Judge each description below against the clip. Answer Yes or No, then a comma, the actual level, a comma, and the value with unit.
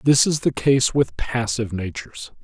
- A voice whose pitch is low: Yes, low, 125 Hz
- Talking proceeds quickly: No, average, 175 wpm